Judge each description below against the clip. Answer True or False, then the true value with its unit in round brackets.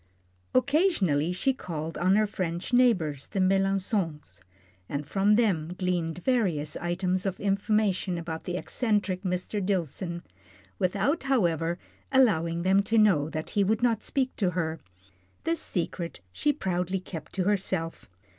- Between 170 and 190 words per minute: False (135 wpm)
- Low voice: False (185 Hz)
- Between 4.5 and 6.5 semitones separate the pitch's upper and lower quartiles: False (3.8 semitones)